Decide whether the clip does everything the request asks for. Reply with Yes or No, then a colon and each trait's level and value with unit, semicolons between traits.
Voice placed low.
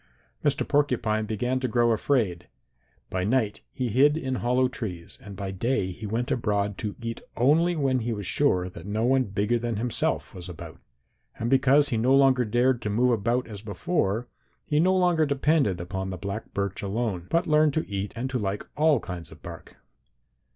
Yes: low, 115 Hz